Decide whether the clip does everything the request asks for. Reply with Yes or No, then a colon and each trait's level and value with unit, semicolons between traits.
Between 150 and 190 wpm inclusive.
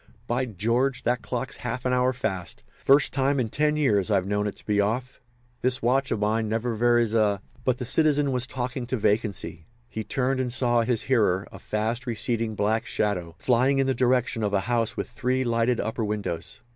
No: average, 200 wpm